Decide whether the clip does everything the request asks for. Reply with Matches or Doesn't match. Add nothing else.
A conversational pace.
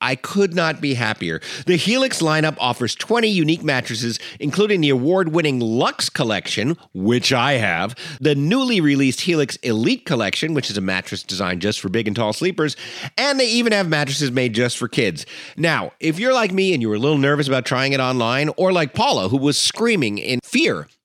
Matches